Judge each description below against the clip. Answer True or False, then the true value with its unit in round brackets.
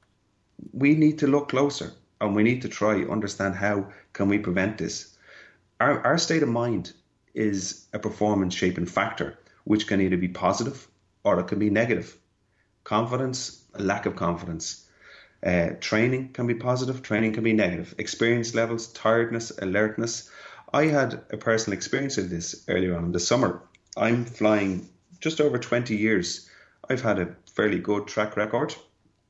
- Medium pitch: False (110 Hz)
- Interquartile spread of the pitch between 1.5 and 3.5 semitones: True (3.1 semitones)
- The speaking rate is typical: True (165 wpm)